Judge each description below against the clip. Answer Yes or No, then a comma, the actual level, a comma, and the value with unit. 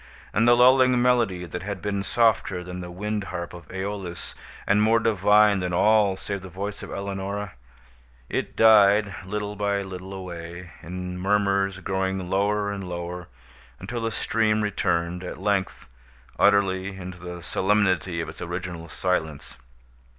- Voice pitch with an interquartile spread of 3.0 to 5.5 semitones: No, narrow, 2.5 semitones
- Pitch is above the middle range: No, very low, 95 Hz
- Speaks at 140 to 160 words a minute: Yes, average, 150 wpm